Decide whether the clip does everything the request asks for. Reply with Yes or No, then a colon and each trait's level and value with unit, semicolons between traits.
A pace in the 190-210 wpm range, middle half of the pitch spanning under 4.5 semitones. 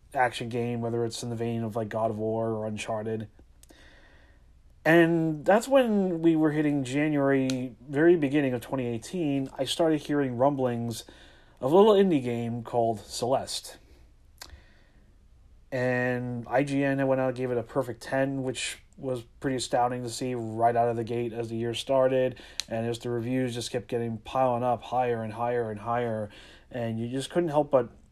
No: average, 175 wpm; average, 2.8 semitones